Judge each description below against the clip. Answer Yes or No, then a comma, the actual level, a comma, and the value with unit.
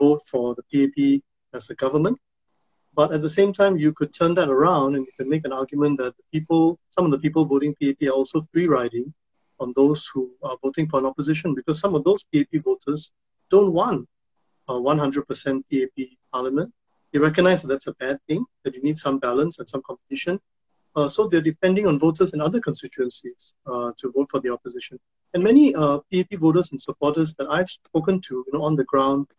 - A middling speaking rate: No, fast, 210 wpm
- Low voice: No, medium, 145 Hz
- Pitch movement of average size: Yes, average, 3.6 semitones